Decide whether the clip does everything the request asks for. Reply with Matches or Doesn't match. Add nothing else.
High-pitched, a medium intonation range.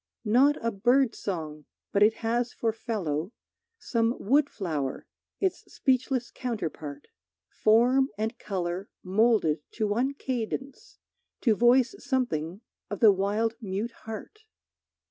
Matches